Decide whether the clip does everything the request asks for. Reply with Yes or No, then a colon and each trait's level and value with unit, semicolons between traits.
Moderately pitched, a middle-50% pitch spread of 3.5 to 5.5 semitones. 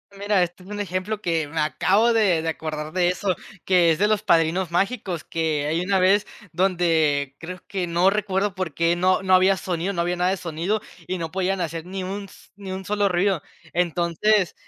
No: medium, 180 Hz; average, 2.7 semitones